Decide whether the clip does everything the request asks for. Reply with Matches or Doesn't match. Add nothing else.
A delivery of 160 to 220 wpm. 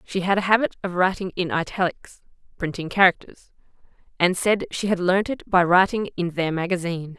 Matches